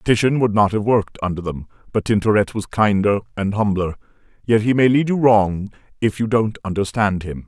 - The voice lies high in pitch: No, low, 105 Hz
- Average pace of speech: Yes, average, 195 wpm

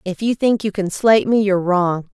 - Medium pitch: No, high, 200 Hz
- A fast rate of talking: Yes, fast, 250 wpm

